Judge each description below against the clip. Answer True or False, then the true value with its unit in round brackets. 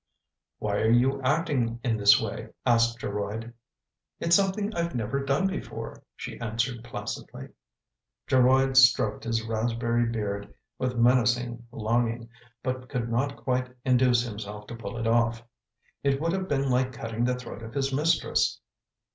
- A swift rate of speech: False (155 wpm)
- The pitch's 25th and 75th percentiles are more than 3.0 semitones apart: False (2.5 semitones)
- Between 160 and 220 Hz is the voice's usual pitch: False (120 Hz)